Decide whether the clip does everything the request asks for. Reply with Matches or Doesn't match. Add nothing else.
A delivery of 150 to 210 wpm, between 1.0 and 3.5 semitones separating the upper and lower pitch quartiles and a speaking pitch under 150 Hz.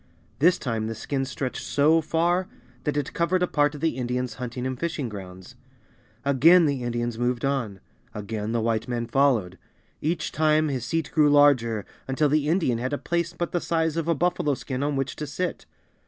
Doesn't match